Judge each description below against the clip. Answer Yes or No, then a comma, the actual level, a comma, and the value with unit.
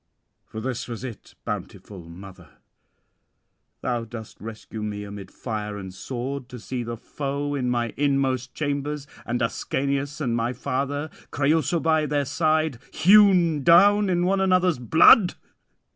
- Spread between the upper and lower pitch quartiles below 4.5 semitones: No, average, 5.0 semitones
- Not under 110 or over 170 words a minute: Yes, average, 140 wpm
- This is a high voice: No, low, 135 Hz